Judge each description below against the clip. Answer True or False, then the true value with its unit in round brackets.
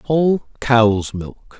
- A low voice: True (125 Hz)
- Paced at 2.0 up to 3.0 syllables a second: True (2.8 syllables/s)